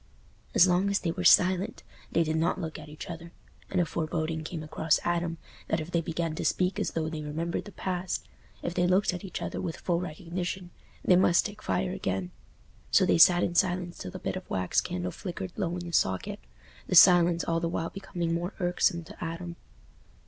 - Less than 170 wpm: No, fast, 205 wpm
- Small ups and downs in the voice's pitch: Yes, narrow, 1.8 semitones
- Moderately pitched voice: Yes, medium, 170 Hz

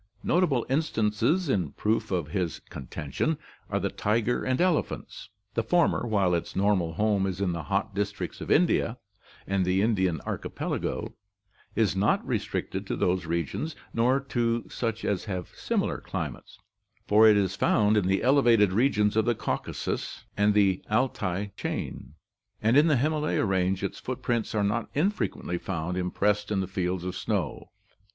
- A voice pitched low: Yes, low, 105 Hz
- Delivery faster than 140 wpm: Yes, average, 160 wpm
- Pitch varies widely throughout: No, average, 4.1 semitones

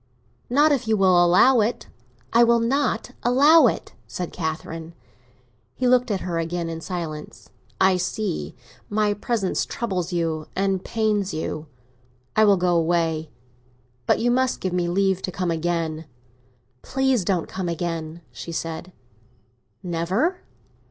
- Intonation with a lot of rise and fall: No, average, 4.9 semitones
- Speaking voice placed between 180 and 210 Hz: Yes, medium, 185 Hz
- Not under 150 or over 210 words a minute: No, average, 140 wpm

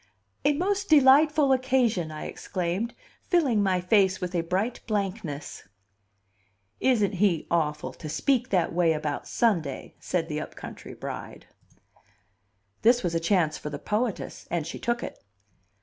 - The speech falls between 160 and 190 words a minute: No, average, 145 wpm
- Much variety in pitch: Yes, wide, 6.8 semitones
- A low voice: No, high, 195 Hz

